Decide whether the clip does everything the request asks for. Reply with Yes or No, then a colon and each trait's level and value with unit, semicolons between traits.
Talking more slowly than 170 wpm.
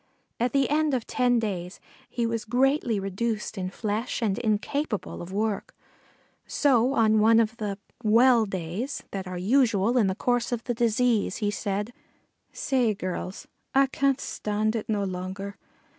Yes: average, 160 wpm